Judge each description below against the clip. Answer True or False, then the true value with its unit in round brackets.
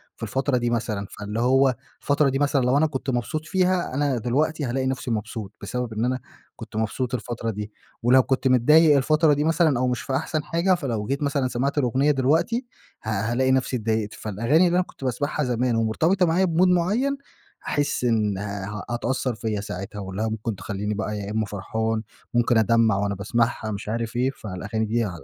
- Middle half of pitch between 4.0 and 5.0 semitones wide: True (4.7 semitones)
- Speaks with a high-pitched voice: False (125 Hz)